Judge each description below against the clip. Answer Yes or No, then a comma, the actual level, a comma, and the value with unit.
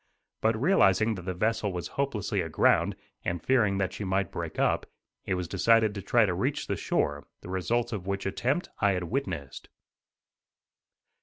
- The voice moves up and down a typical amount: Yes, average, 3.7 semitones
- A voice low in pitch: Yes, low, 100 Hz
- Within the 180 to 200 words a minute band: No, average, 170 wpm